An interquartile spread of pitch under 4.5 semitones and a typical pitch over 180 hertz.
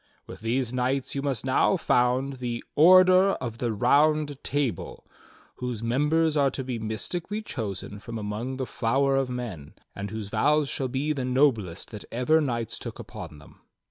No: average, 4.1 semitones; low, 130 Hz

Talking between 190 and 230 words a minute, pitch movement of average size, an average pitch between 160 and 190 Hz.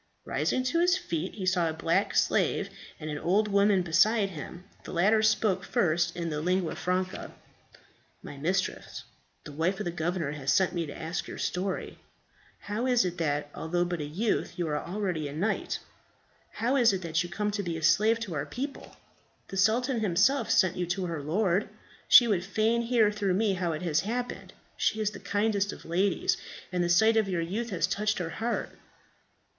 Yes: average, 195 wpm; average, 4.1 semitones; medium, 185 Hz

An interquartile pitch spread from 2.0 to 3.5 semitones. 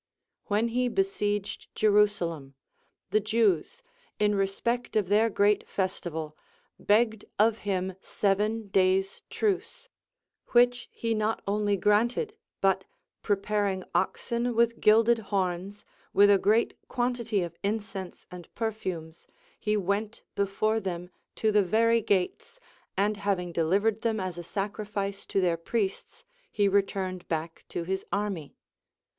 Yes: average, 2.7 semitones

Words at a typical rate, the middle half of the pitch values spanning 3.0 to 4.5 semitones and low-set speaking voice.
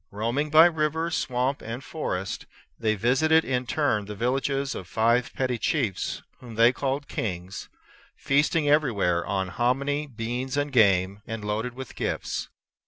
No: average, 145 wpm; average, 4.9 semitones; low, 125 Hz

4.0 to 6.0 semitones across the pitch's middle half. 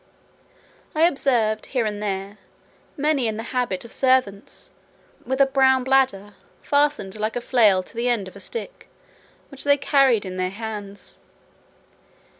Yes: average, 4.7 semitones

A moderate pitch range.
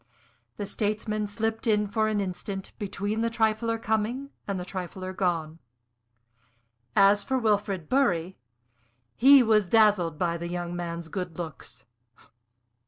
Yes: average, 3.7 semitones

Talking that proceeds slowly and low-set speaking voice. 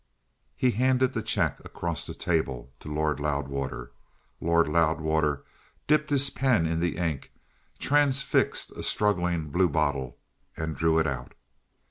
Yes: slow, 130 wpm; very low, 80 Hz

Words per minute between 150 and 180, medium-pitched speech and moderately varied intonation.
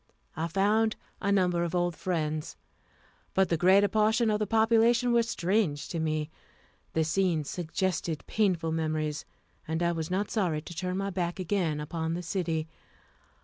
Yes: average, 160 wpm; medium, 175 Hz; average, 3.9 semitones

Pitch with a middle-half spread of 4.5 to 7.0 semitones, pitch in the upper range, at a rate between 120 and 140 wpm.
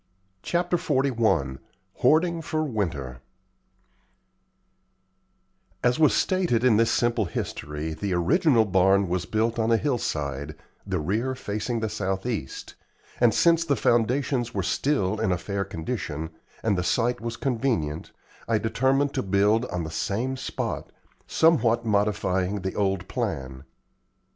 No: wide, 5.5 semitones; low, 110 Hz; slow, 135 wpm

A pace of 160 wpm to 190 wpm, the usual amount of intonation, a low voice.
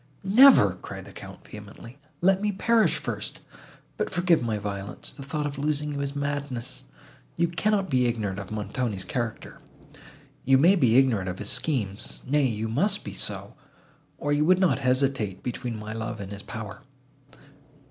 No: average, 165 wpm; wide, 5.9 semitones; low, 130 Hz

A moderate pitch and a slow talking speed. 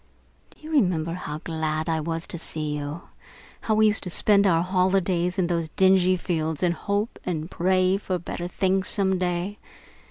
No: medium, 180 Hz; average, 185 wpm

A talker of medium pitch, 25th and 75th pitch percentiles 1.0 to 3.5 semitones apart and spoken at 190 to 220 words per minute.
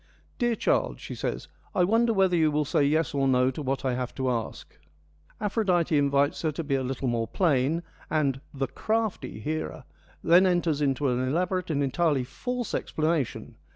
No: medium, 150 Hz; average, 4.8 semitones; average, 200 wpm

